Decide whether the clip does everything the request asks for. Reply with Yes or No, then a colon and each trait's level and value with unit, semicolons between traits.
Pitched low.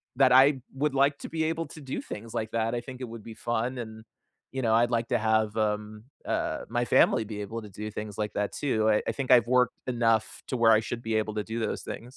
Yes: low, 115 Hz